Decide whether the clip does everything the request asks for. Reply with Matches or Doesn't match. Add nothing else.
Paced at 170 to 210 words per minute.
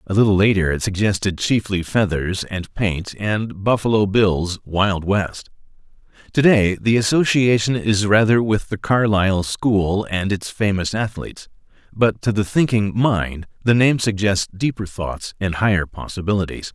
Doesn't match